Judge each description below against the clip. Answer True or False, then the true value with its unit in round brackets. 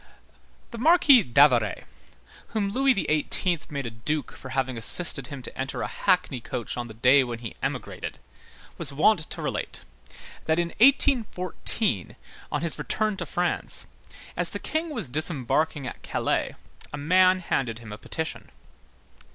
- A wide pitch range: True (6.8 semitones)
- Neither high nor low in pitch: True (155 Hz)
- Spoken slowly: False (150 wpm)